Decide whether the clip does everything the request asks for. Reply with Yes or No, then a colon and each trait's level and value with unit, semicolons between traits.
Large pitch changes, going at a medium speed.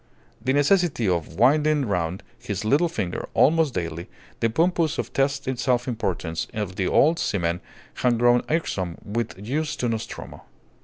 Yes: wide, 7.2 semitones; average, 150 wpm